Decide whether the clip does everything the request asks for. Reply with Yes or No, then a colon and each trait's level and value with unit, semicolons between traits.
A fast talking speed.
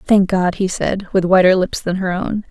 Yes: fast, 240 wpm